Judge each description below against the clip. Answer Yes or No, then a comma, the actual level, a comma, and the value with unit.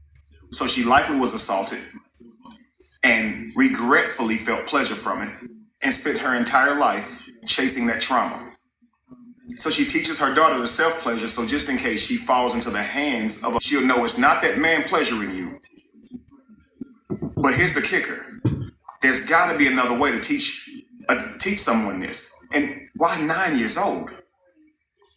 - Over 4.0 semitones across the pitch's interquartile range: Yes, wide, 5.5 semitones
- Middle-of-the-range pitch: No, high, 245 Hz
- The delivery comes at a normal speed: Yes, average, 155 wpm